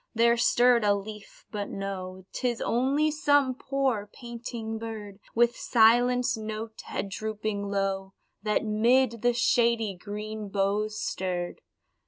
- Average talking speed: No, slow, 125 wpm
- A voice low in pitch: No, high, 220 Hz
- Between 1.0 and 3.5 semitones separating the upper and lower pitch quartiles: Yes, average, 2.8 semitones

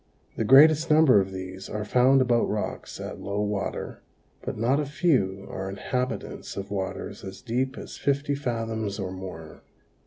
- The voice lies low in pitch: Yes, low, 110 Hz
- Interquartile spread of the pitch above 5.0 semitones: Yes, wide, 5.5 semitones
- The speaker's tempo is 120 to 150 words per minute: No, average, 160 wpm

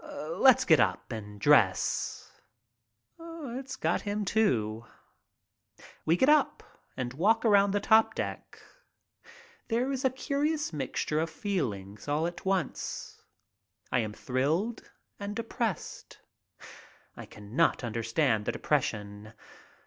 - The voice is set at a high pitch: No, medium, 165 Hz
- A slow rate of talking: Yes, slow, 115 wpm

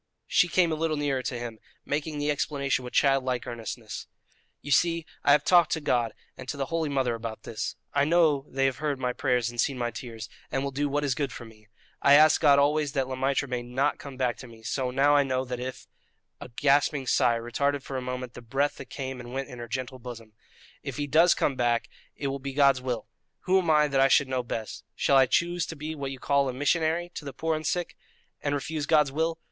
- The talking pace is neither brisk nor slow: No, fast, 245 wpm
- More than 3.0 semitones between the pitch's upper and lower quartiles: No, average, 2.7 semitones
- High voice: No, low, 135 Hz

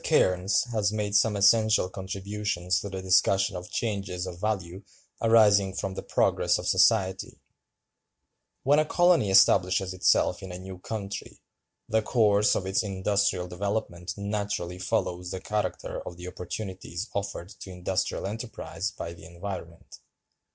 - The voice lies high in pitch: No, very low, 95 Hz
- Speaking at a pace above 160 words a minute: No, average, 140 wpm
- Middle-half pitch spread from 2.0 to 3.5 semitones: Yes, narrow, 2.5 semitones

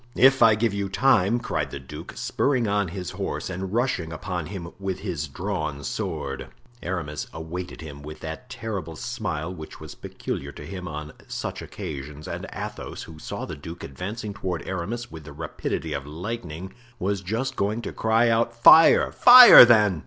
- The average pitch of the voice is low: Yes, very low, 90 Hz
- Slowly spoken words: No, average, 175 wpm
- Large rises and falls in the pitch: Yes, wide, 6.0 semitones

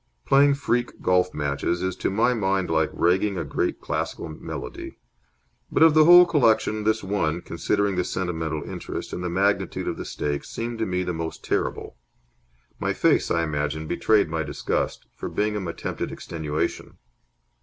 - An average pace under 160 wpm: No, average, 165 wpm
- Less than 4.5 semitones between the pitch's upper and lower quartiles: No, average, 5.1 semitones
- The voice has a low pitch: Yes, very low, 90 Hz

